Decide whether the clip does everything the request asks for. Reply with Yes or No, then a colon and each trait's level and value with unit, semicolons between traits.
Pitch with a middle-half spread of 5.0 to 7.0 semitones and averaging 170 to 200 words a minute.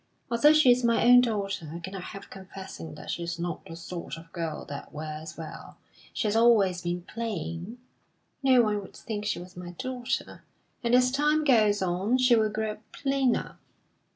Yes: wide, 5.6 semitones; average, 180 wpm